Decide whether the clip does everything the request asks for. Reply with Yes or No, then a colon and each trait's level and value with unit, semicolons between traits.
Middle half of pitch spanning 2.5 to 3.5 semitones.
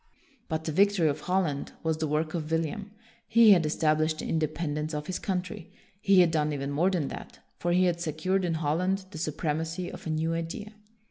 Yes: average, 2.9 semitones